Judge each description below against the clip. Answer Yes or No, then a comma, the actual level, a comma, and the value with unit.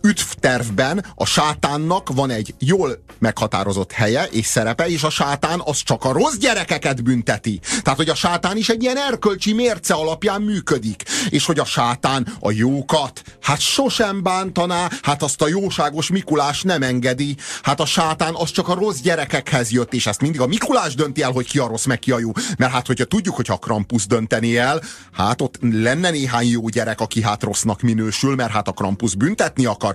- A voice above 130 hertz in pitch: Yes, medium, 140 Hz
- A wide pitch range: Yes, wide, 6.6 semitones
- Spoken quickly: Yes, fast, 190 wpm